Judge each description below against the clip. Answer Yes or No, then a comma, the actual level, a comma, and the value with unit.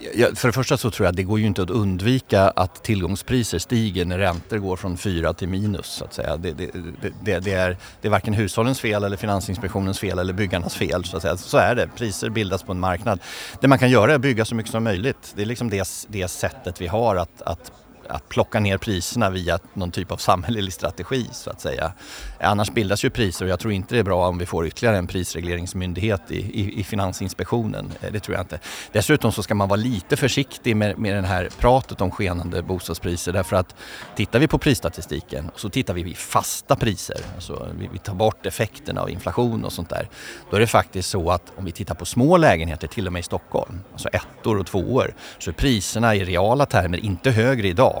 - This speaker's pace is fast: Yes, fast, 230 wpm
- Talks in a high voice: No, low, 100 Hz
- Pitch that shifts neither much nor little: Yes, average, 3.9 semitones